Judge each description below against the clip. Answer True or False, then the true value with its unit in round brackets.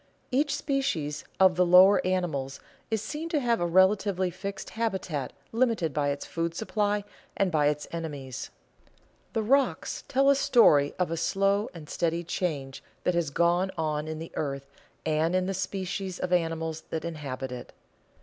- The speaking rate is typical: True (165 wpm)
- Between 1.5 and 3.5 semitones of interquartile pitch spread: False (4.3 semitones)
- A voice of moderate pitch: True (175 Hz)